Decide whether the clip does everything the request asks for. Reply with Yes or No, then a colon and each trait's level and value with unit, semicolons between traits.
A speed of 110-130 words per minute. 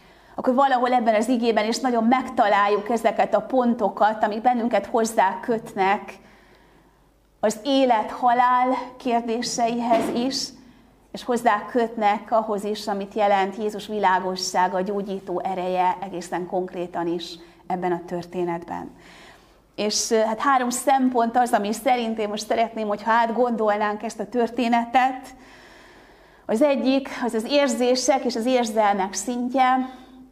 Yes: average, 125 wpm